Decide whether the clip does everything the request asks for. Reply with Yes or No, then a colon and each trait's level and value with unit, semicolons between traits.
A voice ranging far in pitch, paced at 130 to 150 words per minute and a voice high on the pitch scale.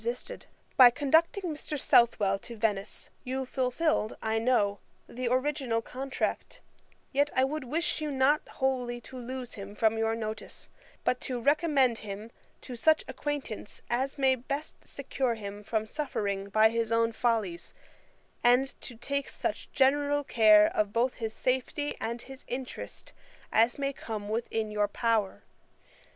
No: average, 3.7 semitones; average, 145 wpm; high, 245 Hz